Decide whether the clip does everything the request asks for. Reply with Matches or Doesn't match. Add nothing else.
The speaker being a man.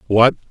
Matches